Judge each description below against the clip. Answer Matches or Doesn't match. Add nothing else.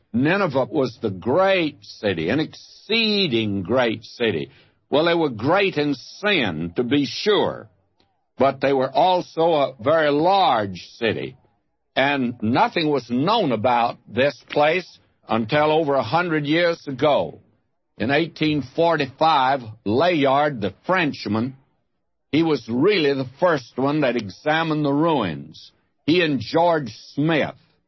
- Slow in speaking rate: Matches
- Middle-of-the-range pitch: Matches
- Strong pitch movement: Doesn't match